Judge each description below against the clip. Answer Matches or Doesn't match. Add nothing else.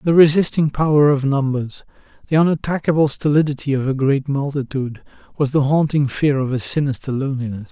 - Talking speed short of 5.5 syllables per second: Doesn't match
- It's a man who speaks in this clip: Matches